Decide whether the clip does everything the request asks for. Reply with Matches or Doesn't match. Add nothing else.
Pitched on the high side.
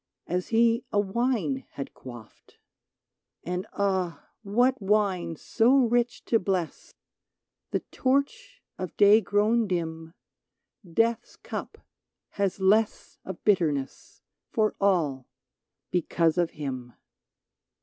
Matches